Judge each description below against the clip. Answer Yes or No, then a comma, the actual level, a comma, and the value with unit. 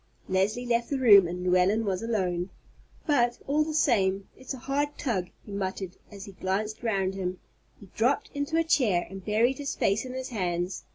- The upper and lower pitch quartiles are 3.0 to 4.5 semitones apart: No, average, 5.3 semitones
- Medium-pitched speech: No, high, 210 Hz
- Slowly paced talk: No, average, 190 wpm